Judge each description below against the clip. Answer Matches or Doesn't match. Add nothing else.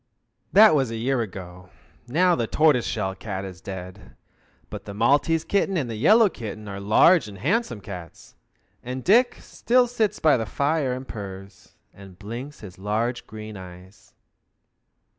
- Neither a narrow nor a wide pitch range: Doesn't match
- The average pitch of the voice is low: Matches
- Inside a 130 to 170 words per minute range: Matches